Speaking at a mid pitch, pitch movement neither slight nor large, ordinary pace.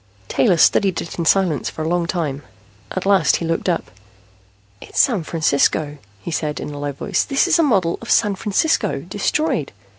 Yes: medium, 175 Hz; average, 4.4 semitones; average, 185 wpm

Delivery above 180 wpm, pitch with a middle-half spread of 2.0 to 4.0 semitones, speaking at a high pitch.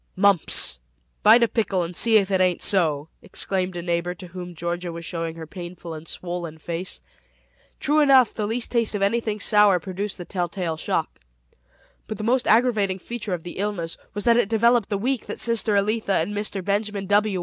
Yes: average, 195 wpm; average, 3.6 semitones; high, 195 Hz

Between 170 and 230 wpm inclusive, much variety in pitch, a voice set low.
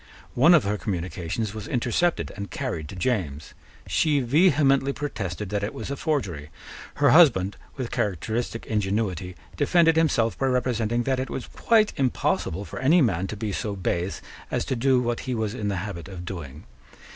Yes: average, 175 wpm; wide, 5.9 semitones; low, 110 Hz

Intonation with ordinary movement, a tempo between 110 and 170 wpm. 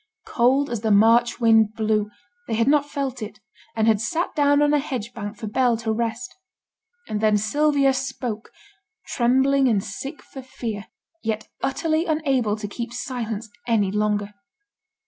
Yes: average, 3.9 semitones; average, 160 wpm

